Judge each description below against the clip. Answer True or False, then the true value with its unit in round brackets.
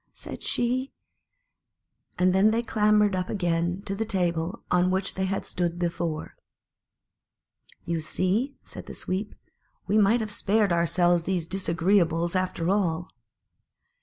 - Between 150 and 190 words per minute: False (135 wpm)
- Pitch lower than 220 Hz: True (185 Hz)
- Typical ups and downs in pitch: True (3.2 semitones)